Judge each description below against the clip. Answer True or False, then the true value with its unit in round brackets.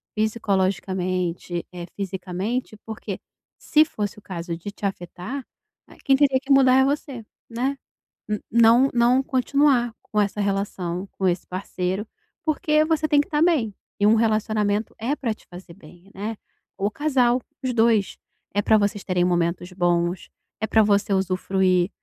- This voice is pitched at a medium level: False (210 Hz)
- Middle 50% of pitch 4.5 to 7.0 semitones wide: True (5.1 semitones)